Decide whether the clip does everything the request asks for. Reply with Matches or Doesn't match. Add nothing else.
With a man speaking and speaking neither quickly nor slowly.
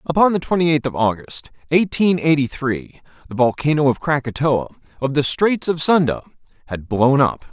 Matches